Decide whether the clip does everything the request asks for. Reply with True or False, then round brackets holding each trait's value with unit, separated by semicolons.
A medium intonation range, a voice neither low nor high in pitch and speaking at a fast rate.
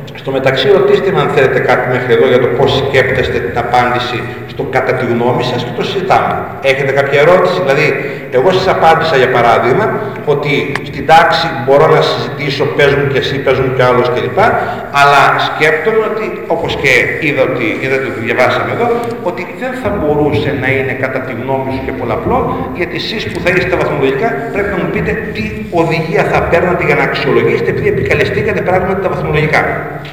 False (6.0 semitones; 145 Hz; 180 wpm)